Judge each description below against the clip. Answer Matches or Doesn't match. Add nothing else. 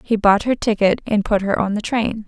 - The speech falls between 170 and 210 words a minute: Doesn't match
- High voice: Matches